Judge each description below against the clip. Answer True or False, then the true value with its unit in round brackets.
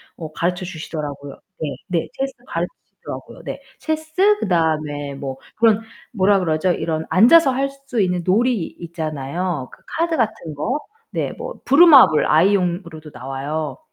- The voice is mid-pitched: True (180 Hz)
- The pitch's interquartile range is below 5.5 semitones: False (8.0 semitones)